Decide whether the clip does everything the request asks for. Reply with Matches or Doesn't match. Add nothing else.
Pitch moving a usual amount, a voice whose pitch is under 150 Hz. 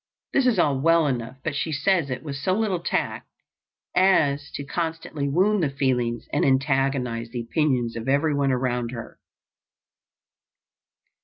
Matches